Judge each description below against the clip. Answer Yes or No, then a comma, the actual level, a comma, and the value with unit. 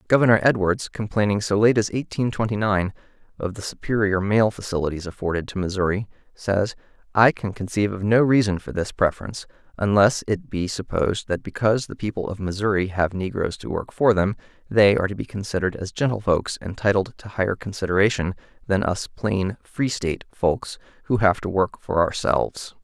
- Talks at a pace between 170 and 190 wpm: Yes, average, 175 wpm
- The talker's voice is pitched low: Yes, low, 100 Hz